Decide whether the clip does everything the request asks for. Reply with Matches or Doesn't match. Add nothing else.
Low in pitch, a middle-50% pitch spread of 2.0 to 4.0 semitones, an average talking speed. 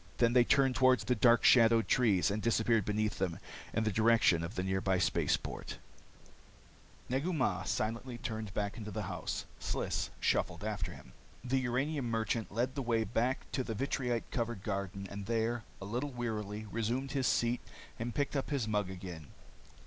Matches